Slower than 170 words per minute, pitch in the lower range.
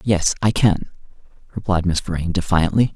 Yes: average, 140 wpm; very low, 90 Hz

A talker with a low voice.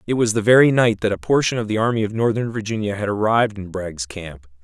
Yes: low, 105 Hz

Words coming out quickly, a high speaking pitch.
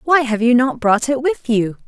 Yes: fast, 255 wpm; high, 240 Hz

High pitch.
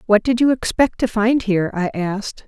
Yes: high, 220 Hz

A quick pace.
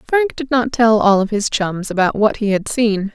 Yes: fast, 250 wpm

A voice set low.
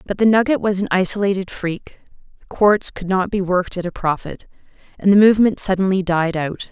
No: high, 190 Hz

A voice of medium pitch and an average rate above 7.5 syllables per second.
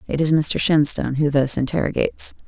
No: medium, 150 Hz; 5.8 syllables/s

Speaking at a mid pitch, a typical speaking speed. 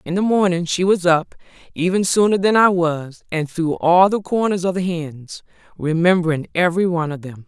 Yes: medium, 175 Hz; average, 195 wpm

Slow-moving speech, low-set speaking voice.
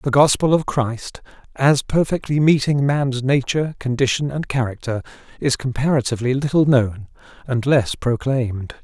Yes: slow, 130 wpm; low, 130 Hz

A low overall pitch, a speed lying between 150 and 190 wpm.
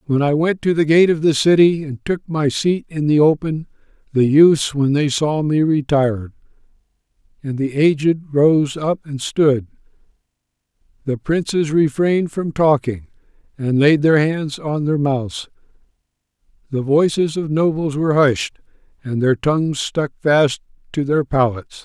No: medium, 150 Hz; average, 155 wpm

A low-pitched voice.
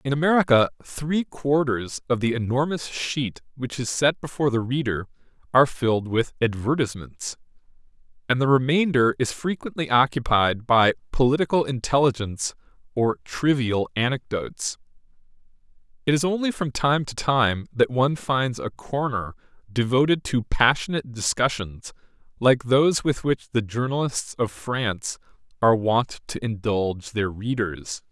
Yes: low, 125 Hz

